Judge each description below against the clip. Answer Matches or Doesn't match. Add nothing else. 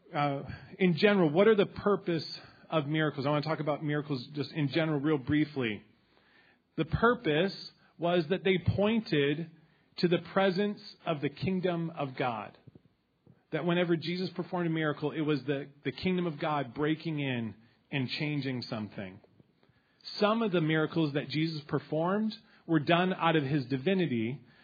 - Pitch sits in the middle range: Matches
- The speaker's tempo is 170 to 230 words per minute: Doesn't match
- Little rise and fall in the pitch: Doesn't match